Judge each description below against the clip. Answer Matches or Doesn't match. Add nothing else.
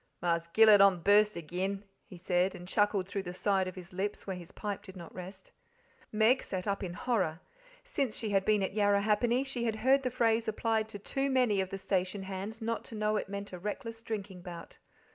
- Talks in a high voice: Matches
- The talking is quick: Matches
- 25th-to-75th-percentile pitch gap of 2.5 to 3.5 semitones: Matches